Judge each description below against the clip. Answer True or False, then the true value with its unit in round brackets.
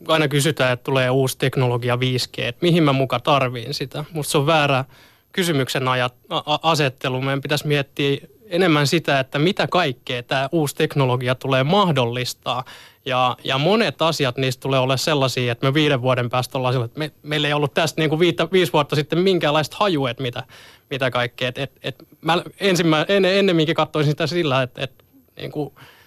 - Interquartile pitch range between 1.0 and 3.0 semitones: False (3.5 semitones)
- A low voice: False (145 Hz)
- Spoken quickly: True (185 wpm)